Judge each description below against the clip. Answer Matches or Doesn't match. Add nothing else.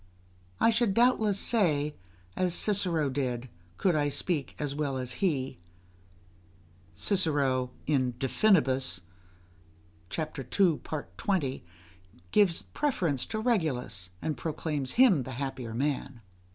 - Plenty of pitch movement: Matches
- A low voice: Doesn't match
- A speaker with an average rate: Doesn't match